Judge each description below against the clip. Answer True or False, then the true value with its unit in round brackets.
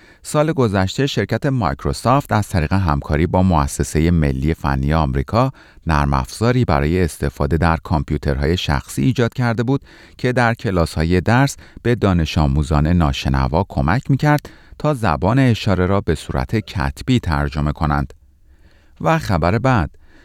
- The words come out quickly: False (130 wpm)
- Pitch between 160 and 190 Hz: False (85 Hz)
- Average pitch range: False (7.7 semitones)